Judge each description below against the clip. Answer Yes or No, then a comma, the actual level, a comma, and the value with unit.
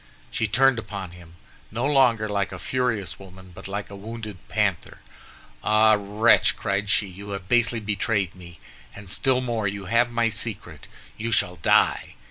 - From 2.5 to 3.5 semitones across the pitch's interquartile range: Yes, average, 2.9 semitones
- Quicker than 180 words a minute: No, average, 165 wpm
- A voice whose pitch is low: Yes, low, 105 Hz